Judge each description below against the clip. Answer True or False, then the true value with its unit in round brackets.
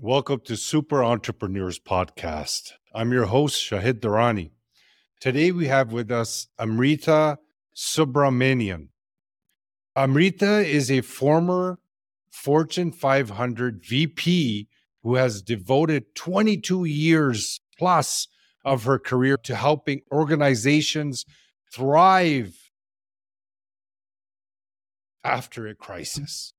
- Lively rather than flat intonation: True (5.9 semitones)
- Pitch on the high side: False (130 Hz)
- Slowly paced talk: True (90 wpm)